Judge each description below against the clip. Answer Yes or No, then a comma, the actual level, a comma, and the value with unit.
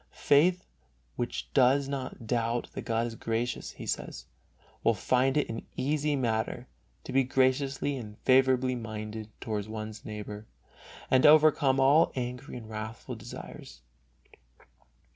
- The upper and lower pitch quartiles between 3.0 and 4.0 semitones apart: Yes, average, 3.3 semitones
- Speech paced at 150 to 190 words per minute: No, slow, 135 wpm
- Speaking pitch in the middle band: No, low, 125 Hz